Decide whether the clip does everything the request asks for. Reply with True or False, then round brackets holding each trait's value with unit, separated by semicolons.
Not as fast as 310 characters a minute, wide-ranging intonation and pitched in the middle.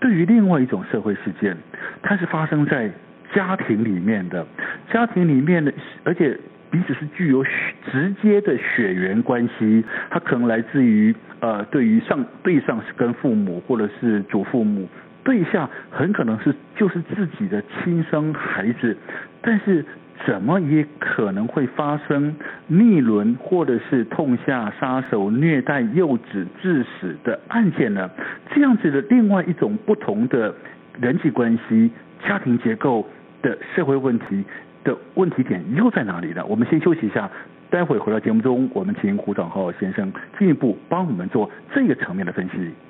True (250 characters per minute; 8.2 semitones; 165 Hz)